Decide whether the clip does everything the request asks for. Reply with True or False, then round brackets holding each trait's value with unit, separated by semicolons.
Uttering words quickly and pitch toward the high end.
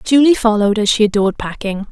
False (190 wpm; 220 Hz)